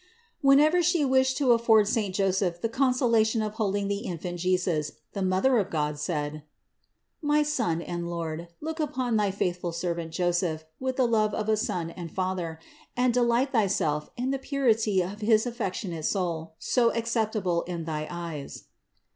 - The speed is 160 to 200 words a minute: Yes, average, 165 wpm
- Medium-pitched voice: No, high, 200 Hz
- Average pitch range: No, wide, 5.8 semitones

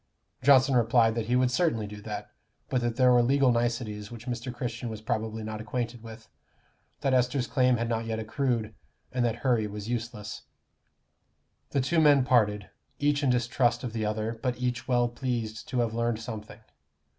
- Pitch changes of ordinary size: No, narrow, 2.2 semitones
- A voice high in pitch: No, low, 120 Hz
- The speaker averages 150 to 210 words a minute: Yes, average, 180 wpm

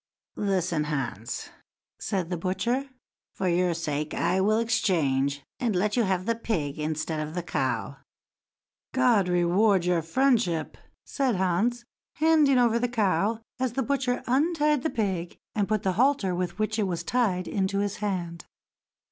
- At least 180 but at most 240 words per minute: No, average, 155 wpm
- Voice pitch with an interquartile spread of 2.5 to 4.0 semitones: No, wide, 5.6 semitones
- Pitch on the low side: No, high, 195 Hz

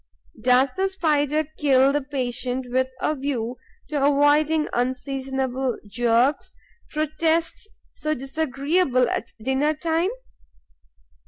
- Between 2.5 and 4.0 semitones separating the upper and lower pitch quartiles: Yes, average, 3.1 semitones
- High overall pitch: Yes, very high, 275 Hz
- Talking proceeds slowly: Yes, slow, 100 wpm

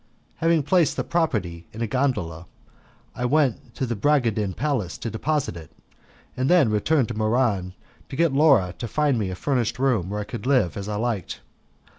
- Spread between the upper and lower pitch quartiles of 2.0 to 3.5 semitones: No, wide, 5.5 semitones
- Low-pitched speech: Yes, low, 120 Hz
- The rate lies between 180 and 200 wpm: Yes, average, 185 wpm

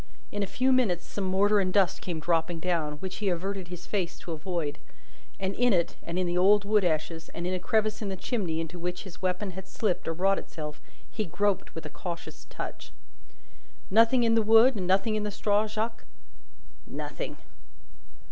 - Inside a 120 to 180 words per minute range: No, average, 195 wpm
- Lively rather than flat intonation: No, average, 3.3 semitones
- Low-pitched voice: No, high, 190 Hz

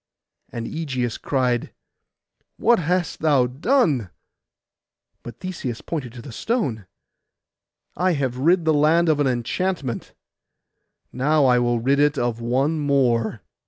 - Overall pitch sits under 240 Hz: Yes, medium, 140 Hz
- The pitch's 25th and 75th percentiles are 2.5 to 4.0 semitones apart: No, average, 4.8 semitones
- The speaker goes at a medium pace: No, slow, 125 wpm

